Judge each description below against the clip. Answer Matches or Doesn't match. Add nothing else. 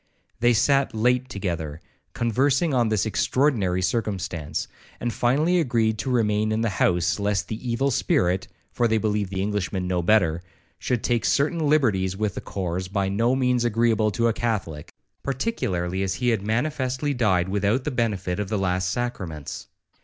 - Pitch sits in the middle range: Doesn't match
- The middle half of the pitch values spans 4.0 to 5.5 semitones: Matches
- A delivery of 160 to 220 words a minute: Matches